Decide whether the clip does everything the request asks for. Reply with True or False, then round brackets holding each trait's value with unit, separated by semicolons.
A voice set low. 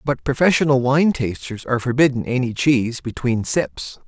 True (125 Hz)